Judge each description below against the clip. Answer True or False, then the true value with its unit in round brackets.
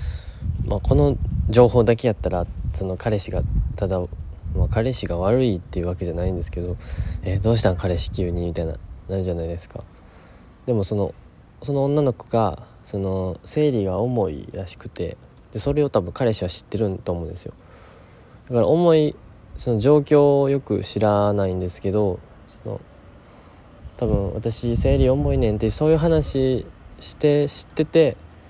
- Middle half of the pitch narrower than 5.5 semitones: True (5.1 semitones)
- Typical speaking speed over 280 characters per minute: True (315 characters per minute)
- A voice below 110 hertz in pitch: True (100 Hz)